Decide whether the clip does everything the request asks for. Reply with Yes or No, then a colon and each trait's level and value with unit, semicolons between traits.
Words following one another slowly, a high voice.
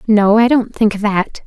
No: fast, 205 wpm; high, 215 Hz